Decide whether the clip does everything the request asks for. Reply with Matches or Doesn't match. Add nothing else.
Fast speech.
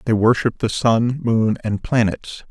Doesn't match